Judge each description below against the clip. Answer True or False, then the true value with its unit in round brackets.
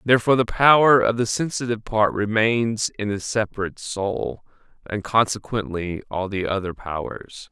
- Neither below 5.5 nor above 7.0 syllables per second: False (5.0 syllables/s)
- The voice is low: True (105 Hz)